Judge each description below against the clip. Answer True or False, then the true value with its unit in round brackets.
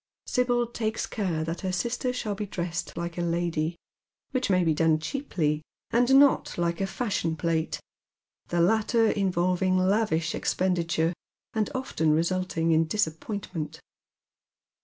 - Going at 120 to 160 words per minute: True (140 wpm)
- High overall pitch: False (180 Hz)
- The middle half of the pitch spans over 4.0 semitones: True (4.7 semitones)